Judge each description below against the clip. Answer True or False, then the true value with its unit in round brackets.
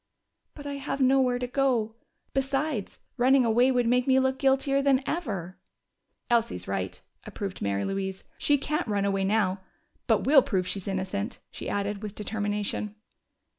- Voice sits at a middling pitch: False (235 Hz)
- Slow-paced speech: False (155 wpm)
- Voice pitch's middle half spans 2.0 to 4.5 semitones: False (5.1 semitones)